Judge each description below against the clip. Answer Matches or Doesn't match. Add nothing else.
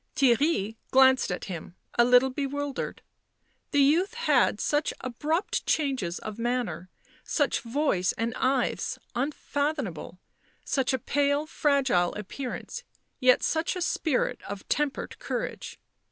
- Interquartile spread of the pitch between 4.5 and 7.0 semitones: Doesn't match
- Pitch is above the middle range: Matches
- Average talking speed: Doesn't match